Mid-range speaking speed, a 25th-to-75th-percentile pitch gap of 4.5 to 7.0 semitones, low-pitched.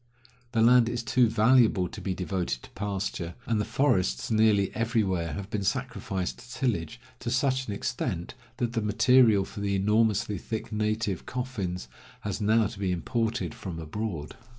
No: average, 165 wpm; average, 3.7 semitones; low, 105 Hz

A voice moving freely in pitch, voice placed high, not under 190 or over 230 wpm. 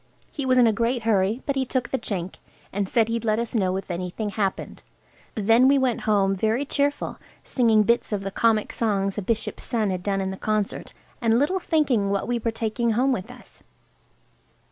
No: average, 3.6 semitones; high, 225 Hz; fast, 205 wpm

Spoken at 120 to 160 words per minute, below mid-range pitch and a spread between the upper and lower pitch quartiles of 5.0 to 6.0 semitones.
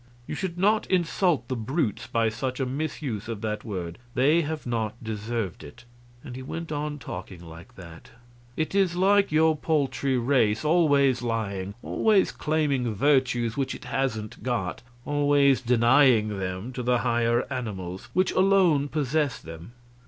Yes: average, 150 wpm; low, 125 Hz; wide, 5.5 semitones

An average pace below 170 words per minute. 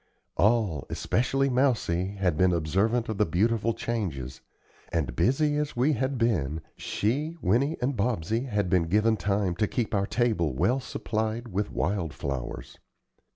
Yes: average, 145 wpm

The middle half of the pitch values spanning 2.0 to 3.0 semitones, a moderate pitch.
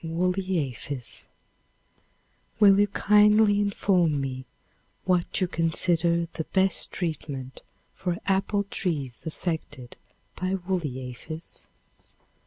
No: average, 4.6 semitones; medium, 175 Hz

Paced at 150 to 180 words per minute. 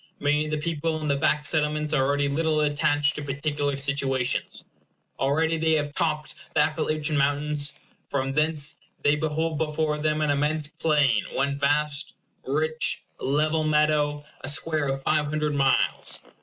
Yes: average, 155 wpm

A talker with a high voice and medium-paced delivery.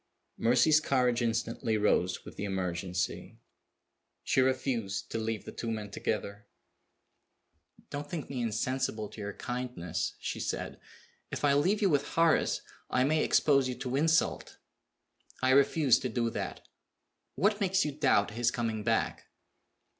No: low, 125 Hz; average, 145 wpm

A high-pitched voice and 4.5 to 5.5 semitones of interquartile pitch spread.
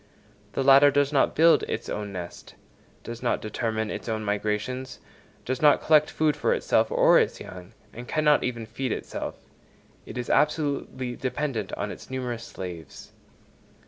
No: low, 125 Hz; average, 4.8 semitones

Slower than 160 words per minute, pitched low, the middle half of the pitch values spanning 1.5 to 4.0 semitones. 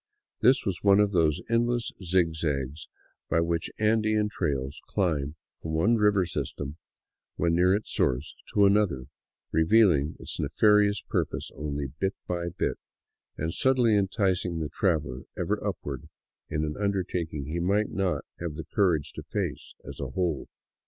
No: average, 150 wpm; very low, 85 Hz; average, 5.1 semitones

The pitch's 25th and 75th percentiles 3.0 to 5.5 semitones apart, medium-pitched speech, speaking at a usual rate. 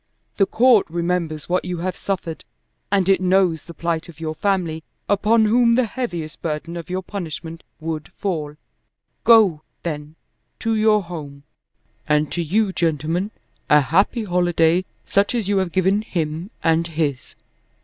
Yes: average, 3.7 semitones; medium, 175 Hz; average, 150 wpm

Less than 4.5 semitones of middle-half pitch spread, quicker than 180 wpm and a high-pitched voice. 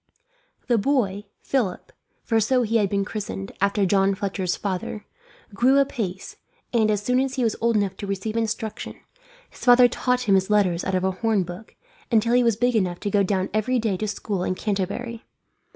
Yes: average, 3.4 semitones; average, 195 wpm; high, 210 Hz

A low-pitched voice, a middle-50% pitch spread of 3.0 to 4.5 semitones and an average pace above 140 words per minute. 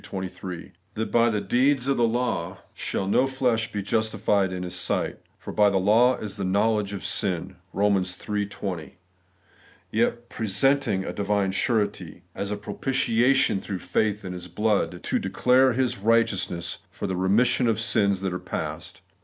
Yes: low, 105 Hz; average, 3.5 semitones; average, 180 wpm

